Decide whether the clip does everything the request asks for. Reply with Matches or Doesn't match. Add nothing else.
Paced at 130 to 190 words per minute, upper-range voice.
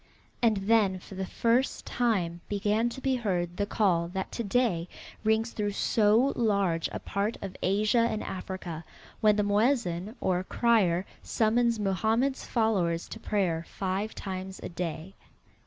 Matches